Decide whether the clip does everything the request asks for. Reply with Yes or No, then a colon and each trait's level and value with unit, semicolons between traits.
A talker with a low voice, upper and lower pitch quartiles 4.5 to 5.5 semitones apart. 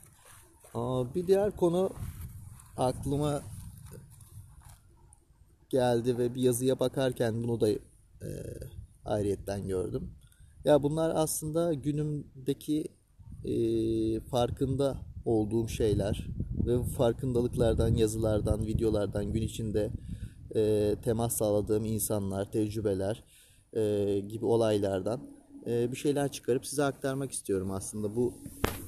No: low, 115 Hz; average, 3.9 semitones